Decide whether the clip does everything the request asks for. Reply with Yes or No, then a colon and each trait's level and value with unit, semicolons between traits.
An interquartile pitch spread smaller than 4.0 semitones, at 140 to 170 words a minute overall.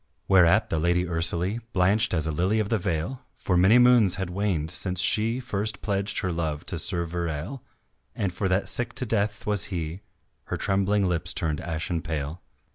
No: average, 3.5 semitones; average, 185 wpm